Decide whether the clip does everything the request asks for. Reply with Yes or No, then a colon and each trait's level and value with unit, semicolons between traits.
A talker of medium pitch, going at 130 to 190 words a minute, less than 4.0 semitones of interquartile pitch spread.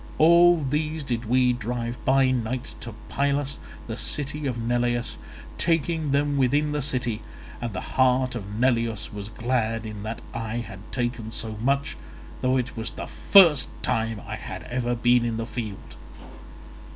No: low, 125 Hz; average, 160 wpm; average, 3.4 semitones